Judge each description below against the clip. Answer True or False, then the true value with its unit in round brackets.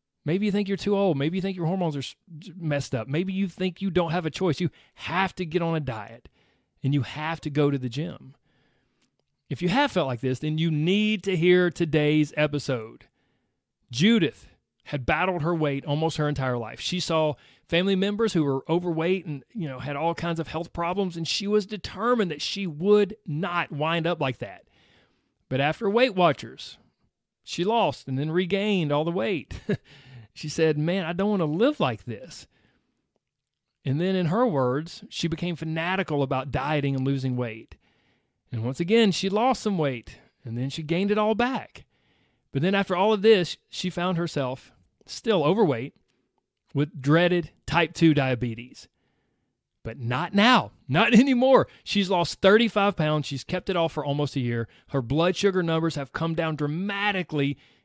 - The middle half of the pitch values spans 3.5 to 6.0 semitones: True (4.9 semitones)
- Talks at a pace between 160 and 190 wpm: True (185 wpm)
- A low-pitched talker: False (165 Hz)